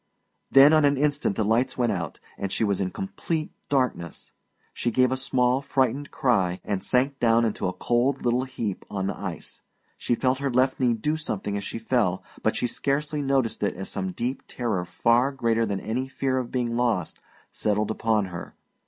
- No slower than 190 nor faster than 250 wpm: Yes, average, 195 wpm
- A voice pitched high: No, low, 120 Hz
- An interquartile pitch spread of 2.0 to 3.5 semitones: No, average, 4.3 semitones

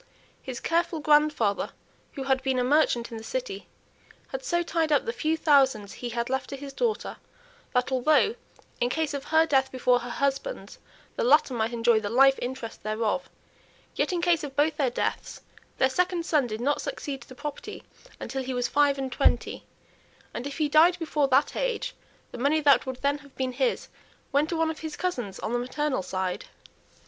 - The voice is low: No, very high, 275 Hz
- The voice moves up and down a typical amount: Yes, average, 4.0 semitones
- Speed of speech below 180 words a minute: No, average, 195 wpm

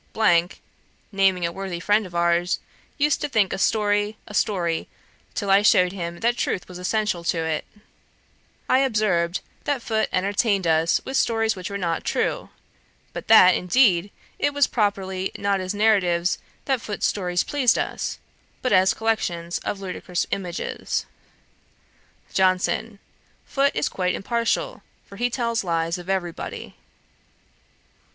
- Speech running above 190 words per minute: No, average, 145 wpm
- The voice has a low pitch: No, high, 195 Hz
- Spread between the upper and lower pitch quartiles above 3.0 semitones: Yes, average, 3.7 semitones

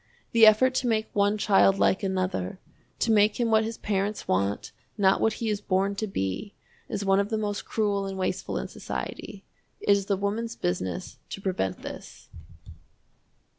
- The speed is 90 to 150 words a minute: No, average, 175 wpm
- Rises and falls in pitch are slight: Yes, narrow, 2.1 semitones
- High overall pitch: Yes, high, 200 Hz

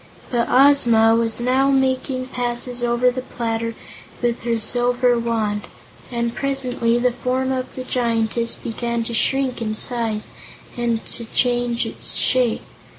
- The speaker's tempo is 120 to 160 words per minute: Yes, average, 140 wpm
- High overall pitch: Yes, high, 240 Hz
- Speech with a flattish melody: Yes, narrow, 1.6 semitones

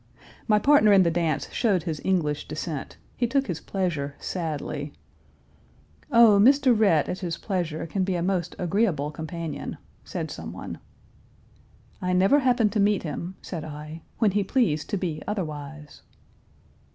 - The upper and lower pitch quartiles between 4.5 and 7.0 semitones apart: Yes, average, 5.0 semitones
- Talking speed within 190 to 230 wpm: No, average, 150 wpm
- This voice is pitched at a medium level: Yes, medium, 180 Hz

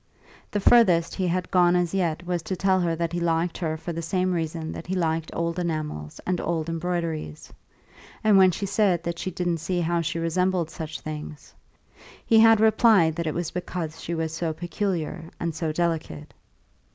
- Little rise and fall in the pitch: Yes, narrow, 2.0 semitones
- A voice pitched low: No, medium, 170 Hz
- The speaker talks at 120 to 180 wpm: No, average, 190 wpm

